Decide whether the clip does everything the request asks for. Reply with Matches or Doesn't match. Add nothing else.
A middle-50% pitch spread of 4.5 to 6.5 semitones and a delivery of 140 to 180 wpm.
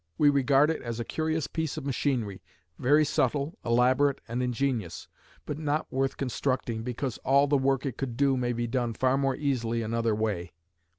Doesn't match